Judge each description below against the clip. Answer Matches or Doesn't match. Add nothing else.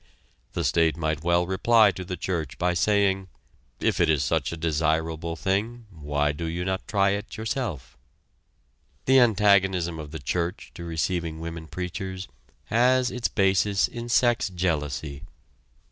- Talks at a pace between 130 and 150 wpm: Matches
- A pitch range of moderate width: Matches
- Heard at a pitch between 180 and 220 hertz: Doesn't match